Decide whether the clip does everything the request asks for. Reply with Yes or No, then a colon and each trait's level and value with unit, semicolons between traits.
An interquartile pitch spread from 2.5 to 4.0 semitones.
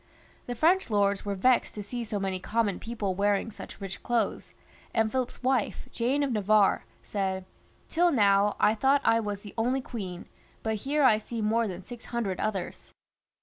Yes: average, 3.4 semitones